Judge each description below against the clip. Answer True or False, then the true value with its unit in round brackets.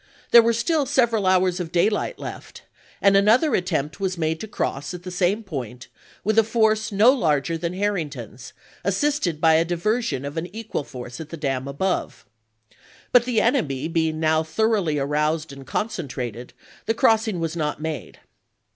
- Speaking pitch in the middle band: True (175 Hz)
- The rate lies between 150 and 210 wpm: True (165 wpm)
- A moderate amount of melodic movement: False (6.2 semitones)